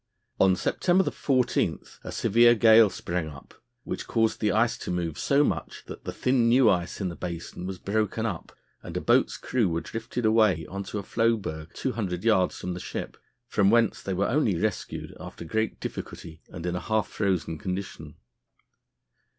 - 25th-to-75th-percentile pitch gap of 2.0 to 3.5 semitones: No, average, 4.4 semitones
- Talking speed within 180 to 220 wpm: Yes, average, 185 wpm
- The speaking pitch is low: Yes, low, 100 Hz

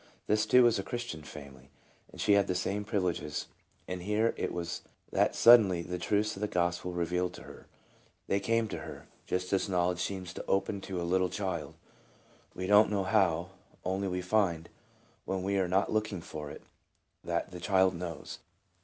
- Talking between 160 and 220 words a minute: Yes, average, 190 wpm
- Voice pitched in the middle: No, very low, 95 Hz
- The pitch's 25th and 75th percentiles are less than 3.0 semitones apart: Yes, narrow, 2.6 semitones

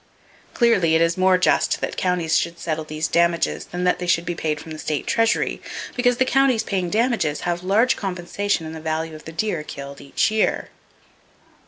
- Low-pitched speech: No, medium, 175 Hz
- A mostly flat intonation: No, average, 4.2 semitones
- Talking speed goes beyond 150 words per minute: Yes, average, 195 wpm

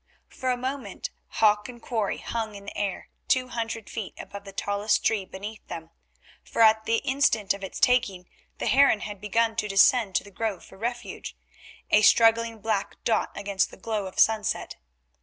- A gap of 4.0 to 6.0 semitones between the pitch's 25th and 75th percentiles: No, narrow, 2.4 semitones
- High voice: Yes, high, 220 Hz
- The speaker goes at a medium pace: Yes, average, 180 wpm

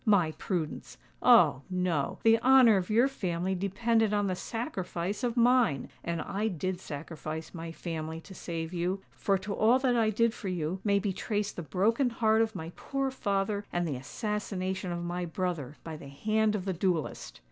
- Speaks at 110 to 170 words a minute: No, average, 180 wpm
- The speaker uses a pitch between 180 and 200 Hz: Yes, high, 190 Hz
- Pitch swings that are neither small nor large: Yes, average, 4.3 semitones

